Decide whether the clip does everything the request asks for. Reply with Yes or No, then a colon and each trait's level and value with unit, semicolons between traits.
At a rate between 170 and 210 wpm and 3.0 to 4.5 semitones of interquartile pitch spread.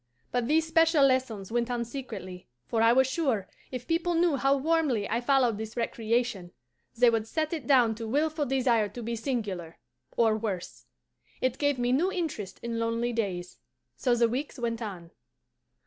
Yes: average, 175 wpm; average, 3.7 semitones